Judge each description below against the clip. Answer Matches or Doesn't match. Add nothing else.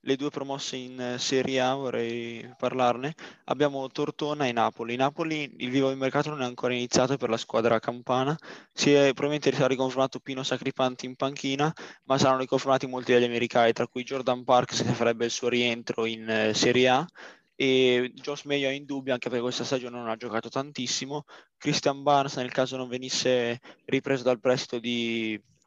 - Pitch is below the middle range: Matches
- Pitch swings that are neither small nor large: Doesn't match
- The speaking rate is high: Matches